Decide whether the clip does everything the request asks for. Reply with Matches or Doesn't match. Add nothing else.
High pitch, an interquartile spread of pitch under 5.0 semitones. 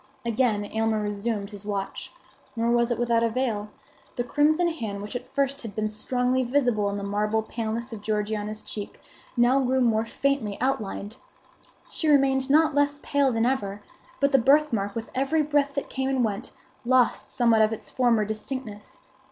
Matches